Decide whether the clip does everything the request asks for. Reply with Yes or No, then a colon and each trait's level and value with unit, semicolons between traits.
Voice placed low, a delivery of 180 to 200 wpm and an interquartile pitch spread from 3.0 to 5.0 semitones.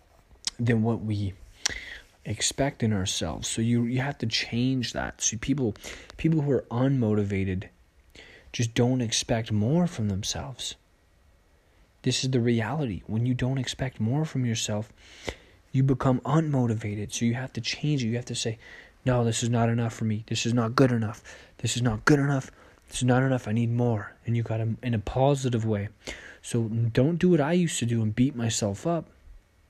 Yes: low, 115 Hz; average, 190 wpm; average, 3.5 semitones